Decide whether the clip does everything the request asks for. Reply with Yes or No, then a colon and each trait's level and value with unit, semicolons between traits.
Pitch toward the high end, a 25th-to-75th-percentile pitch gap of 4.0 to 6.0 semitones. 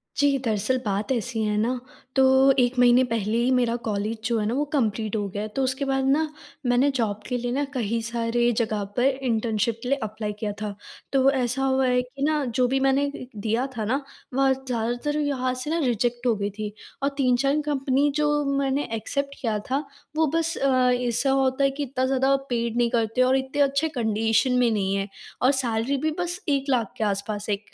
No: very high, 250 Hz; average, 3.3 semitones